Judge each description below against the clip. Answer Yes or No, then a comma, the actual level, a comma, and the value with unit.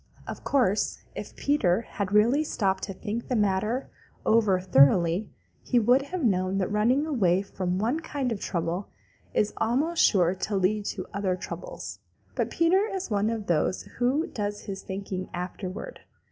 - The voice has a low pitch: No, high, 205 Hz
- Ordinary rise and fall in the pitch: Yes, average, 4.9 semitones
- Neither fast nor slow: Yes, average, 160 wpm